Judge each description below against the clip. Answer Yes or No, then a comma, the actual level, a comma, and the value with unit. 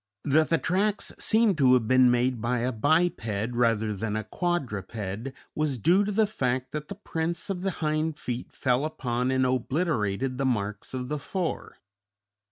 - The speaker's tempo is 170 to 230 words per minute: Yes, average, 175 wpm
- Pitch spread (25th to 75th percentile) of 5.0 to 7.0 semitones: Yes, wide, 5.5 semitones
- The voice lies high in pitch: No, low, 130 Hz